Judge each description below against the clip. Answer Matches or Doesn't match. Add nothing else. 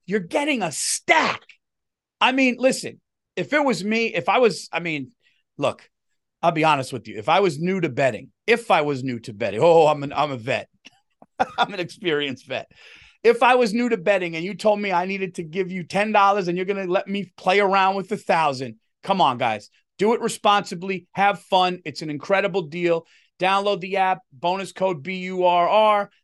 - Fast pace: Matches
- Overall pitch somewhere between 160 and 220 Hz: Matches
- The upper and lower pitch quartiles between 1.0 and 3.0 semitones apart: Doesn't match